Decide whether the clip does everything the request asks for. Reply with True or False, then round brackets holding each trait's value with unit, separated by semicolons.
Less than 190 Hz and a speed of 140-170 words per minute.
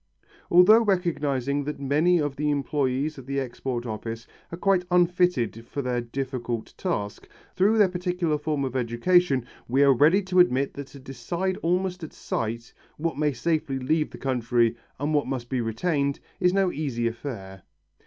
True (140 Hz; 165 wpm)